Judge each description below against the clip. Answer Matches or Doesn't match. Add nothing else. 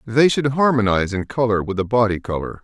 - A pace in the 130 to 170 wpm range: Doesn't match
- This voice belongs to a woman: Doesn't match